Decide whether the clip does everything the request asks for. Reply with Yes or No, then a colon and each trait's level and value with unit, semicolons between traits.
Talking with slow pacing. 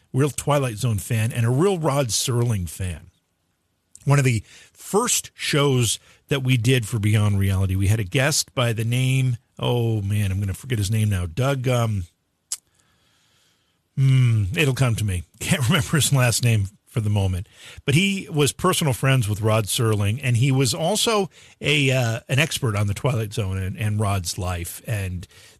No: average, 180 wpm